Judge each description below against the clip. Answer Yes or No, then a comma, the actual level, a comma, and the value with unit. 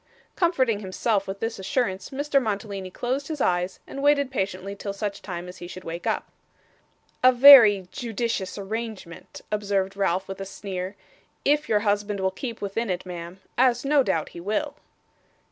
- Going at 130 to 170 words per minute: Yes, average, 165 wpm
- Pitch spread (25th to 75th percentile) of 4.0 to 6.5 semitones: Yes, average, 4.4 semitones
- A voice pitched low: No, high, 205 Hz